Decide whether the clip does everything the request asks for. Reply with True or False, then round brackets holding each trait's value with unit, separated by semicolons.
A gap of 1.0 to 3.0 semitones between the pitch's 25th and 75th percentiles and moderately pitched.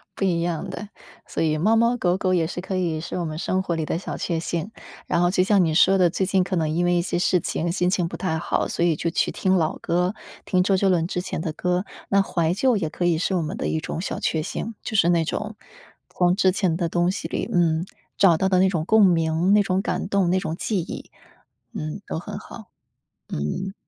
True (2.5 semitones; 180 Hz)